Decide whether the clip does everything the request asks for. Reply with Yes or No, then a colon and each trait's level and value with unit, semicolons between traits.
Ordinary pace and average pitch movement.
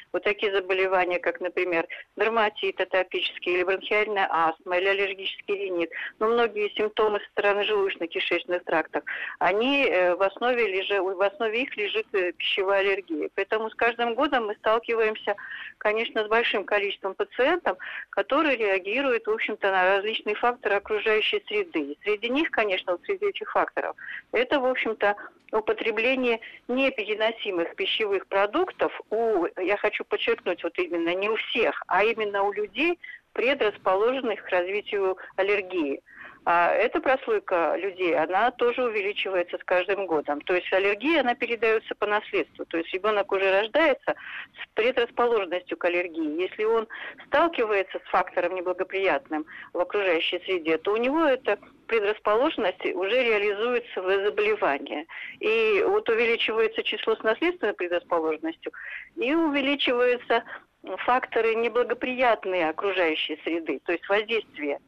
No: average, 130 wpm; wide, 6.5 semitones